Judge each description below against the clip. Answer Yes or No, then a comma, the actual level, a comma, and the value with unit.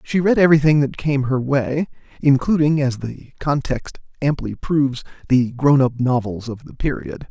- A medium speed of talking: Yes, average, 165 wpm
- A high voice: No, low, 135 Hz